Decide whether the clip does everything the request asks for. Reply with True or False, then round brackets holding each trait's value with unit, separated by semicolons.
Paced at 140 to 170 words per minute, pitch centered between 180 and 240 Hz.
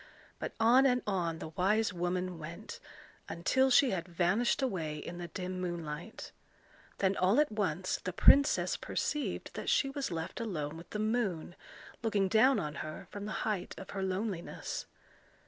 True (165 wpm; 185 Hz)